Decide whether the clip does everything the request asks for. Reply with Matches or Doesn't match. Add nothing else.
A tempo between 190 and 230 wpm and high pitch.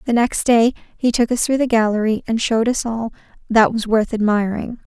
Matches